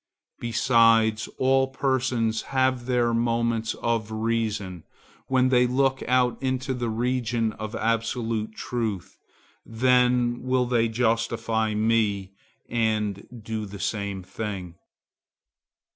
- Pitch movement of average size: No, narrow, 2.3 semitones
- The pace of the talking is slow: Yes, slow, 105 wpm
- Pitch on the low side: Yes, low, 115 Hz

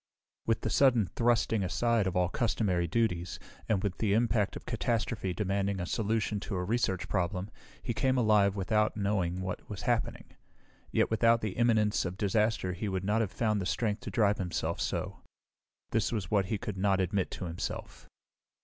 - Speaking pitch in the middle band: No, low, 105 Hz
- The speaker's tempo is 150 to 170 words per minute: No, average, 180 wpm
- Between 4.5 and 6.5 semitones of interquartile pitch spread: No, average, 3.2 semitones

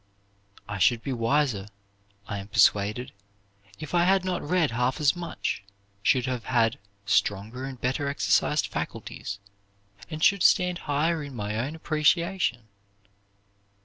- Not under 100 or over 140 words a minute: Yes, slow, 135 wpm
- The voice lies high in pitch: No, low, 130 Hz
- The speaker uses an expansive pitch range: Yes, wide, 6.0 semitones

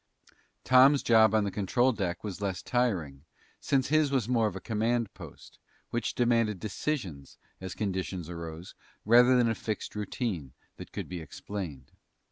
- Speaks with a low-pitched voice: Yes, low, 105 Hz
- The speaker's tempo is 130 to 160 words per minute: Yes, average, 155 wpm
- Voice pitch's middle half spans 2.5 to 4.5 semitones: No, average, 5.0 semitones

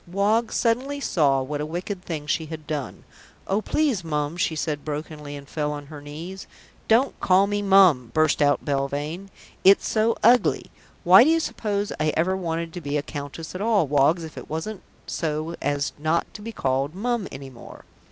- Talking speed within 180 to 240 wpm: Yes, average, 190 wpm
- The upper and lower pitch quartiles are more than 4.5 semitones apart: Yes, average, 5.2 semitones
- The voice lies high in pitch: No, medium, 160 Hz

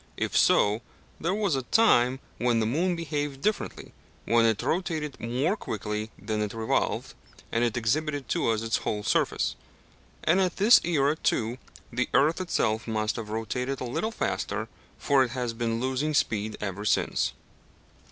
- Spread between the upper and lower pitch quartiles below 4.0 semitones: No, wide, 5.5 semitones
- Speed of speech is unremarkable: Yes, average, 160 wpm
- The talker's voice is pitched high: No, low, 125 Hz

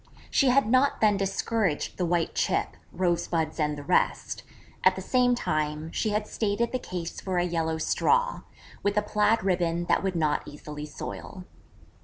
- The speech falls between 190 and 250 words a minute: No, average, 170 wpm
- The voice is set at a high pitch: No, medium, 180 Hz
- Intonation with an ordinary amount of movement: Yes, average, 4.8 semitones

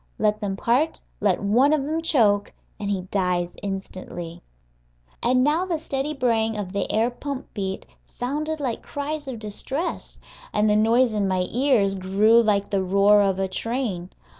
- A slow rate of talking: No, average, 165 wpm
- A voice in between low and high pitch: No, high, 215 Hz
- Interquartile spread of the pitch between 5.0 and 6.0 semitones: Yes, average, 5.3 semitones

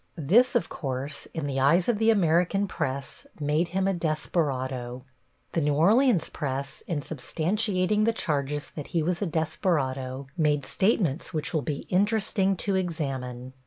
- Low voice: No, medium, 160 Hz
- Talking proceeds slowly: No, average, 155 wpm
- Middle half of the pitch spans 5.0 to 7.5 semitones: Yes, average, 5.3 semitones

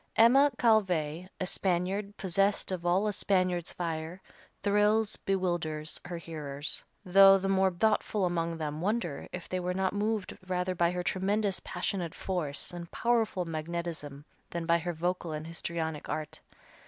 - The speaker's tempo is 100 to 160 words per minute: Yes, average, 150 wpm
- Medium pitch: Yes, medium, 180 Hz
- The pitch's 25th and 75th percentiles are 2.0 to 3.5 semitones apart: Yes, average, 2.7 semitones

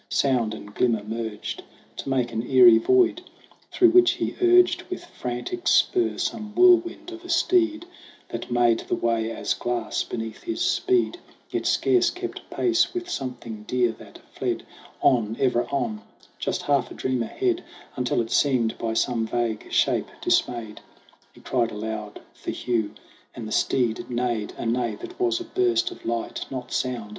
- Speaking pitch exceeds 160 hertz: No, low, 125 Hz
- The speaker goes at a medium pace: Yes, average, 165 wpm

